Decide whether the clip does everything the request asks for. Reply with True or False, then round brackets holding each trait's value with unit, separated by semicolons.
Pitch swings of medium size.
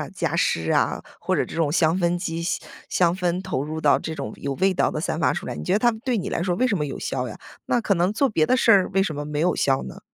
True (3.7 semitones)